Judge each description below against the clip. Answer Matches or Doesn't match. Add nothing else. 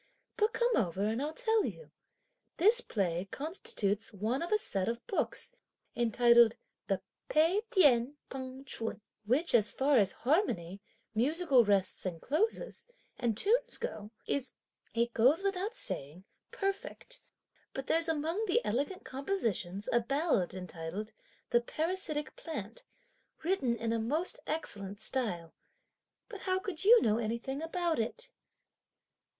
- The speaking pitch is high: Matches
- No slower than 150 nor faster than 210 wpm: Doesn't match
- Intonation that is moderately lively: Doesn't match